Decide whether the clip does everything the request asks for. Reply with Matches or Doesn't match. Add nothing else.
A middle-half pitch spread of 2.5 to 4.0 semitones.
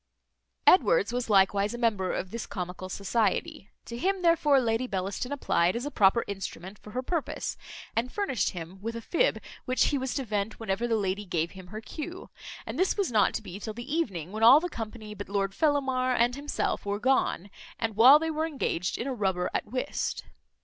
Doesn't match